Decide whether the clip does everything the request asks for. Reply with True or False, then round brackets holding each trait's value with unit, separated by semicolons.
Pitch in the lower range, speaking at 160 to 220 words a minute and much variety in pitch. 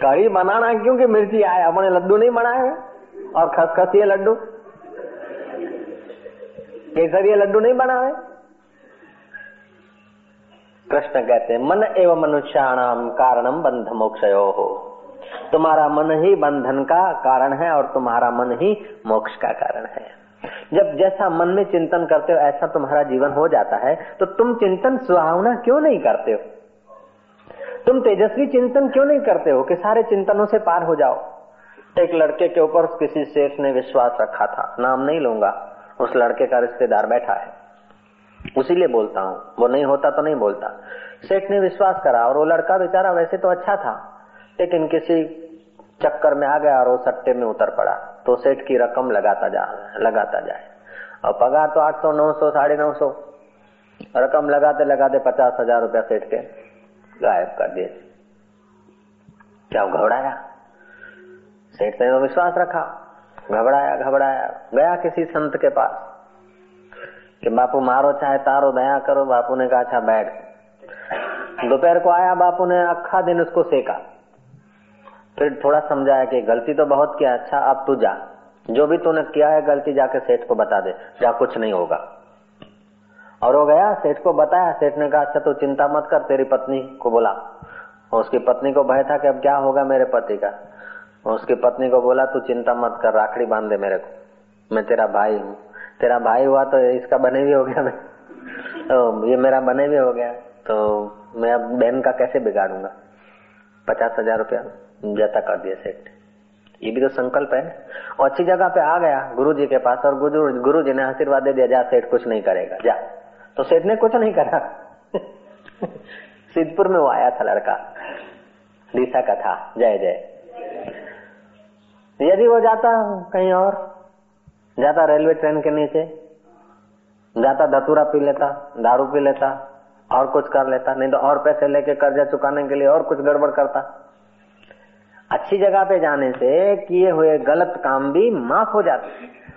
False (150 Hz; 170 wpm; 6.5 semitones)